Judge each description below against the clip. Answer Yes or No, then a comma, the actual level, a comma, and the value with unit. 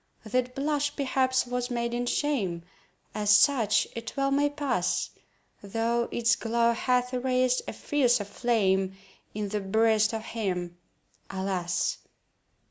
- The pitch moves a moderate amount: Yes, average, 3.7 semitones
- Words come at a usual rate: No, slow, 125 wpm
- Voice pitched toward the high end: Yes, high, 235 Hz